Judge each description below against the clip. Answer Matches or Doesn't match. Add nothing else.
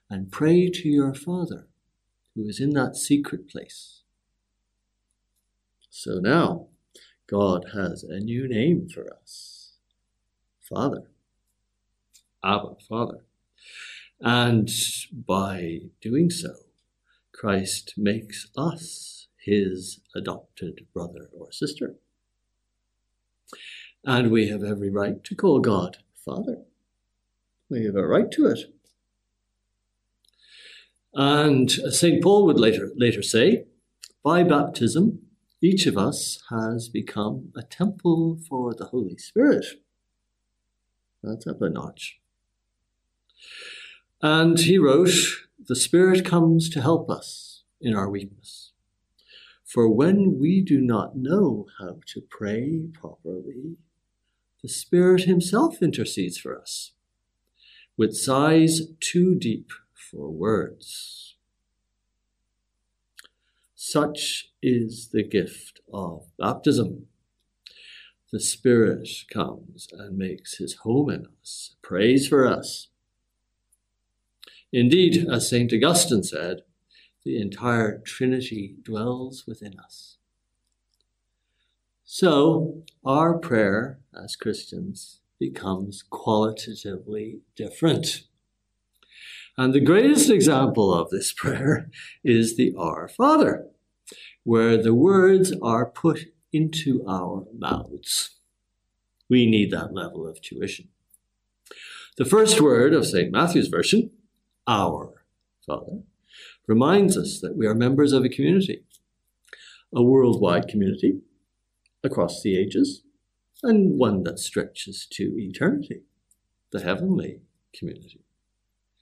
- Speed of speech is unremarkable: Doesn't match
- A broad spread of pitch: Matches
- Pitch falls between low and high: Doesn't match